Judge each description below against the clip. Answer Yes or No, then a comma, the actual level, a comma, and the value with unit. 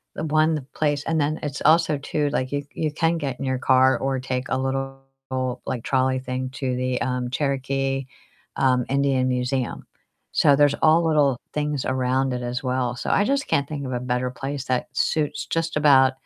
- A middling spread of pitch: No, narrow, 2.3 semitones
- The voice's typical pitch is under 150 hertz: Yes, low, 135 Hz